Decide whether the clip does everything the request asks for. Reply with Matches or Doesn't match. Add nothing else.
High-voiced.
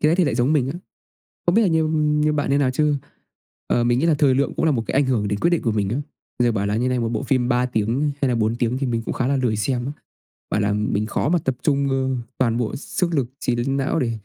Doesn't match